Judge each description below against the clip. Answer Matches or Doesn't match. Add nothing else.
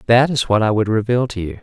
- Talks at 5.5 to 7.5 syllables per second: Matches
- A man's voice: Matches